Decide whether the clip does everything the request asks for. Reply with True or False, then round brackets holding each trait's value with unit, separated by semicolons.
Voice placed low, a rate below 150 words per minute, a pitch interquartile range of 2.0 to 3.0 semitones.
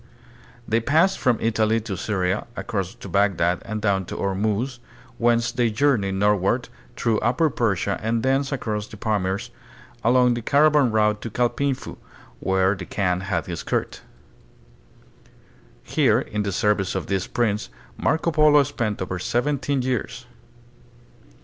False (110 Hz; 140 wpm; 4.2 semitones)